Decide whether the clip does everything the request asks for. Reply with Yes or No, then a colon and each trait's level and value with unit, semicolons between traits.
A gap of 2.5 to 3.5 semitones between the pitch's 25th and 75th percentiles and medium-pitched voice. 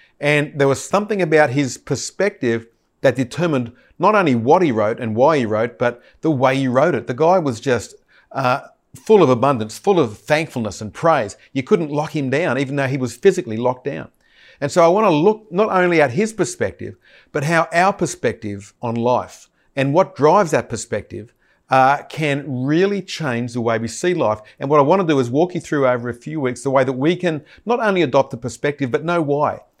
No: average, 5.2 semitones; medium, 145 Hz